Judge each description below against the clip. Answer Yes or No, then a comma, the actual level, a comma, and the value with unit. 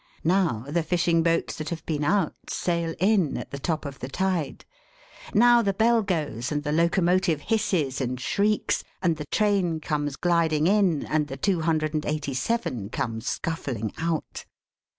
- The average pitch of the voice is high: No, medium, 165 Hz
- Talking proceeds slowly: No, average, 170 wpm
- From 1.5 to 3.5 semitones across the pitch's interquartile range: No, average, 4.1 semitones